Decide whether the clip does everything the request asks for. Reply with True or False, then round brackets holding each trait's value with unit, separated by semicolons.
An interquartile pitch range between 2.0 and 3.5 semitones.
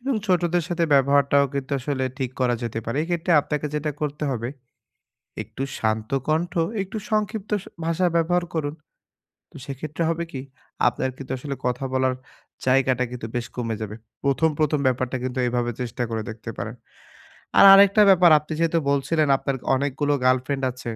False (4.6 semitones)